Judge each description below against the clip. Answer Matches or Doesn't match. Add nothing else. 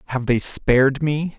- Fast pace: Doesn't match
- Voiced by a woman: Doesn't match